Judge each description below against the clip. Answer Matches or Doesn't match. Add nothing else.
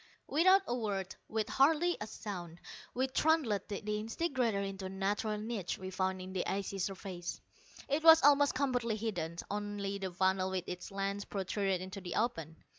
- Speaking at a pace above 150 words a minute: Matches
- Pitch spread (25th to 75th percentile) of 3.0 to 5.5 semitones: Matches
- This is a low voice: Doesn't match